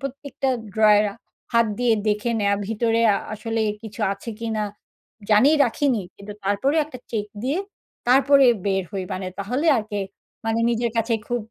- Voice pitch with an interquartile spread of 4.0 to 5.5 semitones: No, average, 3.3 semitones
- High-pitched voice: Yes, high, 225 Hz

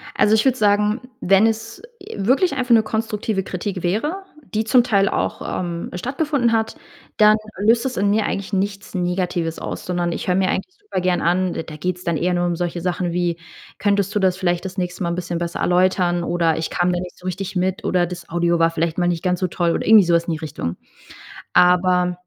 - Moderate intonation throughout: Yes, average, 3.1 semitones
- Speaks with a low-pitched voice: No, medium, 180 Hz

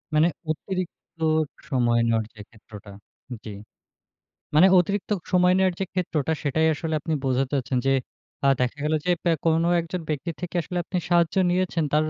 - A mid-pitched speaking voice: Yes, medium, 160 Hz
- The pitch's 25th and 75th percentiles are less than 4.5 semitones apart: No, average, 4.8 semitones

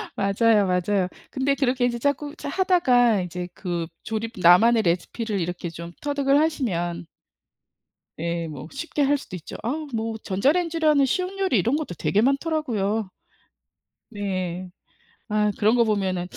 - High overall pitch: Yes, high, 220 Hz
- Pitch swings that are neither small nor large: No, wide, 7.2 semitones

